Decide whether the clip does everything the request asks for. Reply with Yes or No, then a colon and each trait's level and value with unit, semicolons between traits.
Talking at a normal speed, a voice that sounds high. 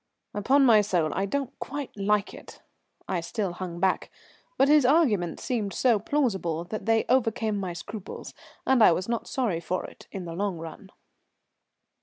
Yes: average, 170 wpm; high, 205 Hz